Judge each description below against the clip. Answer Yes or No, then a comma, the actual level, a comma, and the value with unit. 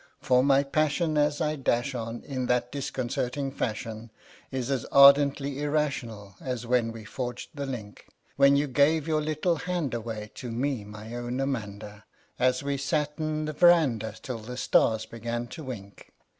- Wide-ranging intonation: No, average, 3.8 semitones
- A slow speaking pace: No, average, 165 wpm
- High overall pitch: No, low, 130 Hz